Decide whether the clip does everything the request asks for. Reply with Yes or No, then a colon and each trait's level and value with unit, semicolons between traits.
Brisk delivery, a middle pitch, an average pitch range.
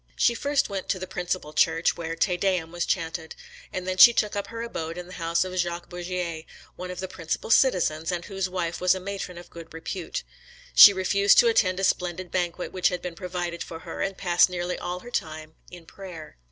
No: fast, 220 wpm; medium, 180 Hz; narrow, 1.8 semitones